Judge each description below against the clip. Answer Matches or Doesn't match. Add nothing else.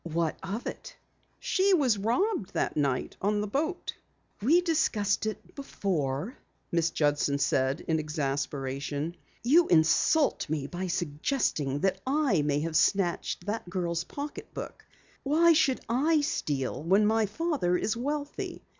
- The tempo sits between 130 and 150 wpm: Matches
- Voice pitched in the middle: Doesn't match